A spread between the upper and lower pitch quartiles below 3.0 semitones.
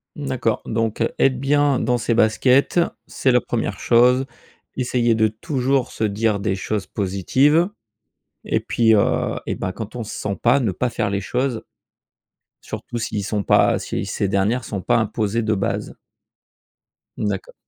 No: average, 3.3 semitones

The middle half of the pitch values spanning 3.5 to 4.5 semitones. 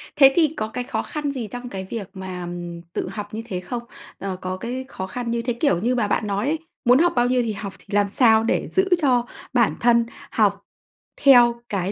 Yes: average, 4.1 semitones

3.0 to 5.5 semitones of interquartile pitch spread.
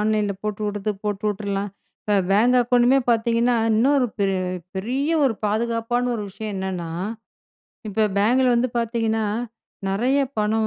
No: narrow, 2.6 semitones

